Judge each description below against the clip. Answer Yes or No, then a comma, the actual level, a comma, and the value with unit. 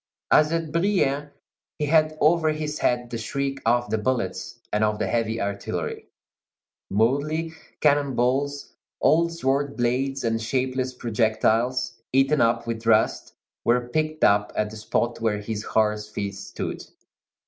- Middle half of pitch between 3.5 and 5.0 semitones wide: Yes, average, 4.5 semitones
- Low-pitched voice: Yes, low, 125 Hz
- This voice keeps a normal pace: Yes, average, 145 wpm